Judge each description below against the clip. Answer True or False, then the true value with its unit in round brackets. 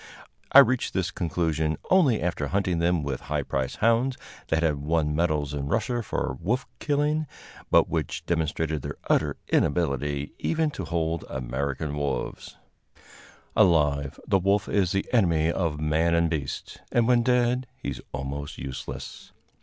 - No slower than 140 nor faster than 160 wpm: True (150 wpm)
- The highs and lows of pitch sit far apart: True (5.9 semitones)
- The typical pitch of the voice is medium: False (80 Hz)